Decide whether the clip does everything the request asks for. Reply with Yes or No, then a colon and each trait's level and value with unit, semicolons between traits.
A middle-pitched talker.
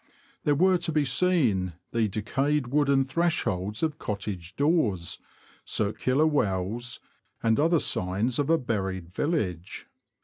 No: low, 125 Hz